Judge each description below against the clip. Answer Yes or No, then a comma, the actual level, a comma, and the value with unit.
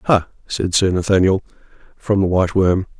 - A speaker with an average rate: Yes, average, 160 wpm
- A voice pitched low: Yes, very low, 95 Hz